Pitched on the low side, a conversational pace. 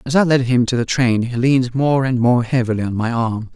No: low, 125 Hz; fast, 270 wpm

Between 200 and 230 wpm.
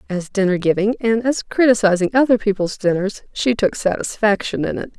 No: average, 170 wpm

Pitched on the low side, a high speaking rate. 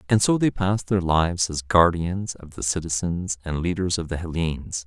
No: very low, 85 Hz; average, 195 wpm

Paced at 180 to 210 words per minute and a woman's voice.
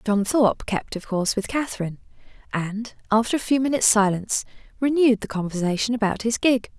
No: average, 170 wpm; female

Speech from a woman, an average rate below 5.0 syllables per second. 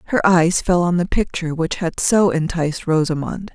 No: female; 5.2 syllables/s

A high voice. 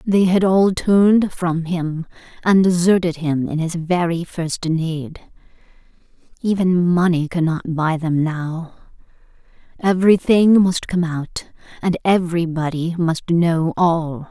No: medium, 170 Hz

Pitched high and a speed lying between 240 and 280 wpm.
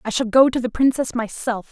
Yes: high, 240 Hz; fast, 245 wpm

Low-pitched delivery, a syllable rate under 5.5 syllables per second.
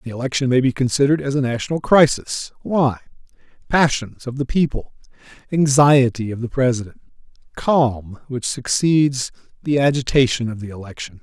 Yes: low, 130 Hz; 5.2 syllables/s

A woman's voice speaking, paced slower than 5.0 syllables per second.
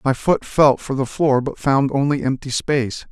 No: male; 4.7 syllables/s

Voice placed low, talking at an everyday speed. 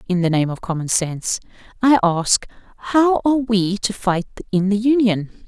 No: high, 205 Hz; average, 175 wpm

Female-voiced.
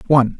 No: male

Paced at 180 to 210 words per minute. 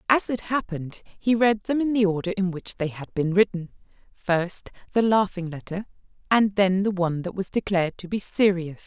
Yes: average, 195 wpm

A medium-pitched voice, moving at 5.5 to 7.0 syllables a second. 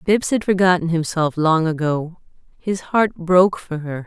No: medium, 170 Hz; 4.5 syllables/s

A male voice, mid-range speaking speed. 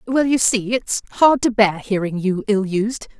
No: female; average, 190 wpm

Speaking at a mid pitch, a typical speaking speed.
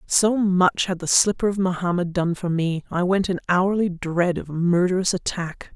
Yes: medium, 180 Hz; average, 190 wpm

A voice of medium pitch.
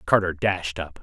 No: very low, 85 Hz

